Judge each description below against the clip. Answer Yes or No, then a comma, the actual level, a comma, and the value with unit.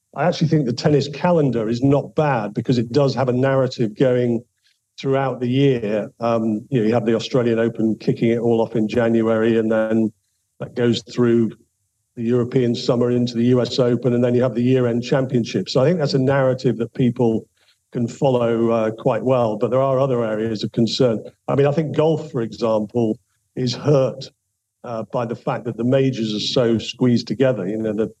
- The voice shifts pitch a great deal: No, average, 2.7 semitones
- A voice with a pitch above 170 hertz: No, low, 120 Hz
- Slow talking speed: No, average, 200 wpm